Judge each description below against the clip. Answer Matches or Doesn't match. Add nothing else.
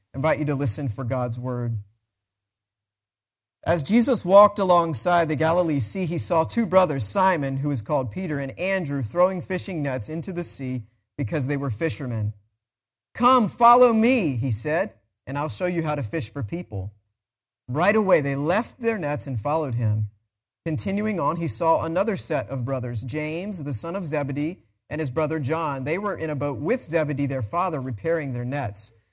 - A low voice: Doesn't match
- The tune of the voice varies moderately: Doesn't match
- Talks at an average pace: Matches